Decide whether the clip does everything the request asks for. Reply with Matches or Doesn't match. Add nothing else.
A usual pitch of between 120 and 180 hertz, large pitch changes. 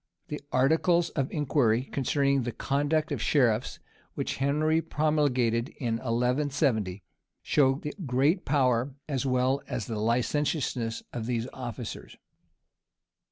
Doesn't match